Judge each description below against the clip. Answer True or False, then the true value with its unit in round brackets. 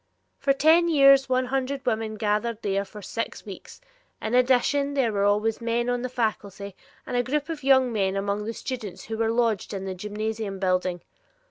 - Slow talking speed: False (195 wpm)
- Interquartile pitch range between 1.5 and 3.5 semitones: False (4.0 semitones)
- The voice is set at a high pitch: True (225 Hz)